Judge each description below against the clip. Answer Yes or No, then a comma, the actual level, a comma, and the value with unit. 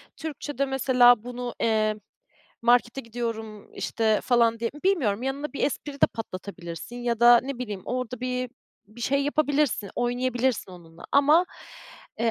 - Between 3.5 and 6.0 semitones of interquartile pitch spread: No, average, 3.1 semitones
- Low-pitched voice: No, high, 245 Hz